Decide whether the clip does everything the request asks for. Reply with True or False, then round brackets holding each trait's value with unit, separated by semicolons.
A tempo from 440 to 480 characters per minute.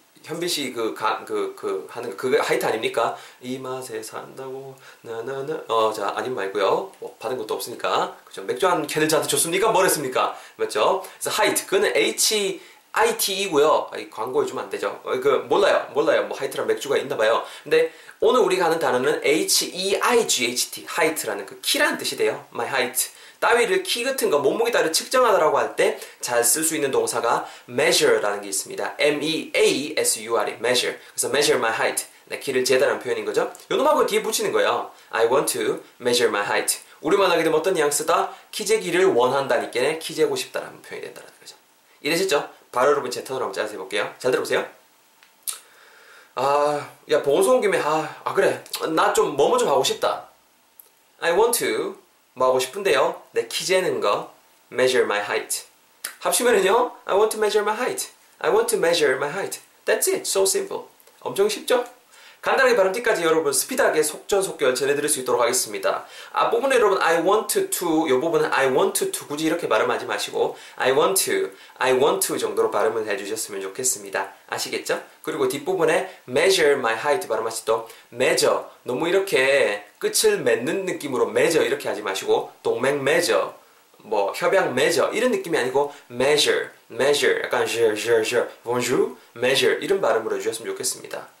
True (455 characters per minute)